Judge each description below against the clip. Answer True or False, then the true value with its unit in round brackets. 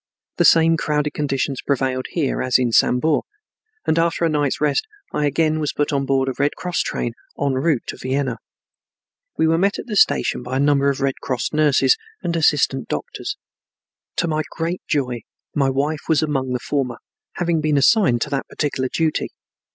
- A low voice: False (145 Hz)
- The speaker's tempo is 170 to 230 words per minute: True (185 wpm)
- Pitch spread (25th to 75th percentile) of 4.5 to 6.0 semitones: False (3.0 semitones)